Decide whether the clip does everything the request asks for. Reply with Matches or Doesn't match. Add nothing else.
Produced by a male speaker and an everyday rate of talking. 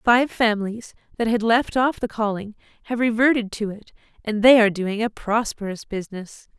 Doesn't match